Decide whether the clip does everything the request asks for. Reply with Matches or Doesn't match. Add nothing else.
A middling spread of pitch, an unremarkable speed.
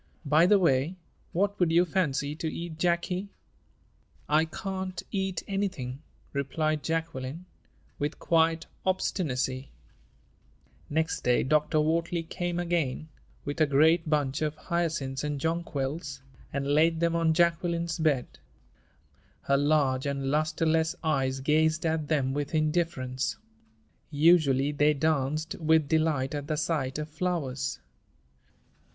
Doesn't match